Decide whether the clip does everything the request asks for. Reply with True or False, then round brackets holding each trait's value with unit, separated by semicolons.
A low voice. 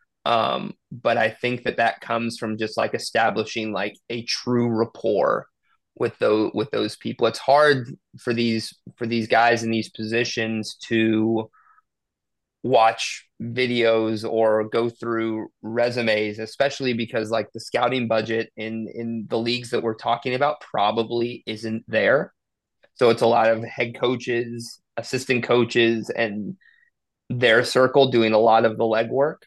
True (115 Hz)